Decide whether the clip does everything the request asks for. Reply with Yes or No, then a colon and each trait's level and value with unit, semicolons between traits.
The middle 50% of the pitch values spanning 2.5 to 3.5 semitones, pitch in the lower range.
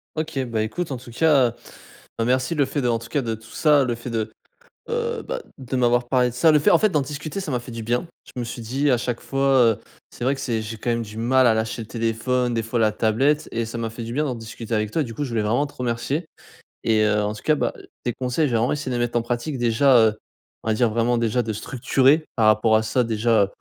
Yes: average, 3.1 semitones; low, 120 Hz